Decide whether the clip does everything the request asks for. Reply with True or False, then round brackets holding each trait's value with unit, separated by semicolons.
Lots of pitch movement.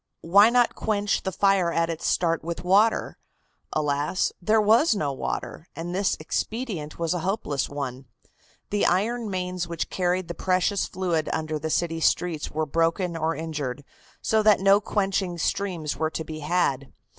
False (3.8 semitones)